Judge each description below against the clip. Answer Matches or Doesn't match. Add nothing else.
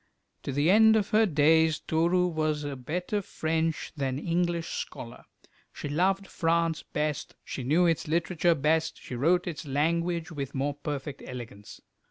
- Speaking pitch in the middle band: Matches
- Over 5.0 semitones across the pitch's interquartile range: Doesn't match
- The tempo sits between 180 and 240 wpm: Doesn't match